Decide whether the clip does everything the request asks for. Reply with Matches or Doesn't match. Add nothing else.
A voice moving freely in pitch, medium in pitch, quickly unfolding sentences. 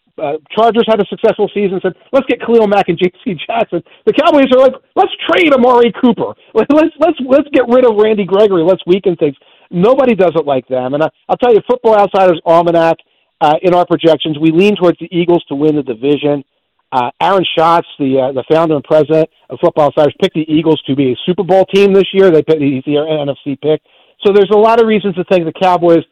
Matches